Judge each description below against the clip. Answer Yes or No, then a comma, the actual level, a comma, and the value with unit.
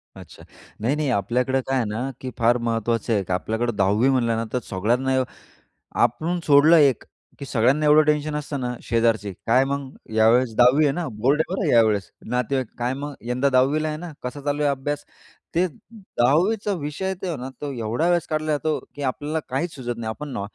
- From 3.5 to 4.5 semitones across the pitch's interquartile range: Yes, average, 4.2 semitones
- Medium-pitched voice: No, low, 130 Hz